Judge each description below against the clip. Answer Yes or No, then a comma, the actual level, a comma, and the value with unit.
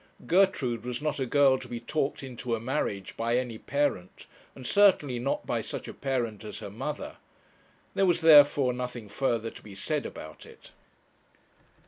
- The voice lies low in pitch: Yes, low, 125 Hz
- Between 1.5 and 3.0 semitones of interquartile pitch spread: No, average, 3.9 semitones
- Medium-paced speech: Yes, average, 170 wpm